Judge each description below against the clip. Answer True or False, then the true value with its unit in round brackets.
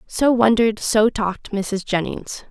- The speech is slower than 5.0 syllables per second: True (4.3 syllables/s)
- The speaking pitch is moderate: False (210 Hz)